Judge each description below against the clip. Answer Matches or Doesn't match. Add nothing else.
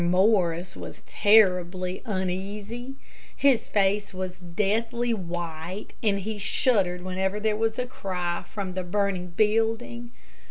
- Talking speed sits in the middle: Doesn't match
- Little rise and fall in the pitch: Doesn't match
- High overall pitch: Matches